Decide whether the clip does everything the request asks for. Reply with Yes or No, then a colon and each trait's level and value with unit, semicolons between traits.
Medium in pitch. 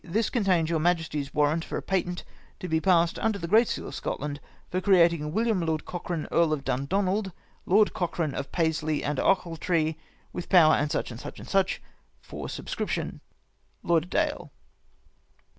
Yes: medium, 170 Hz